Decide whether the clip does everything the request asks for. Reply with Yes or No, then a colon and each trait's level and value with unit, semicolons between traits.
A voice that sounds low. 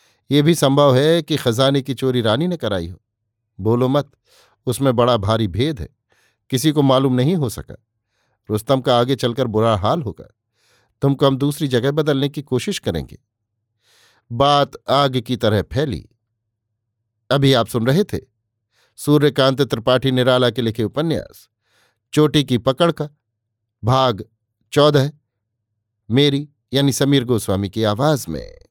Yes: low, 125 Hz